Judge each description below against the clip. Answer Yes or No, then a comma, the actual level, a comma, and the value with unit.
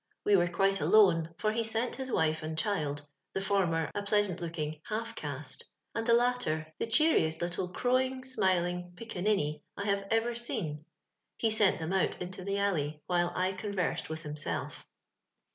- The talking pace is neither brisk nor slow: Yes, average, 180 wpm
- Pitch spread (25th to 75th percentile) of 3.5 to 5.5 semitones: Yes, average, 5.2 semitones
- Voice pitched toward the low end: No, high, 190 Hz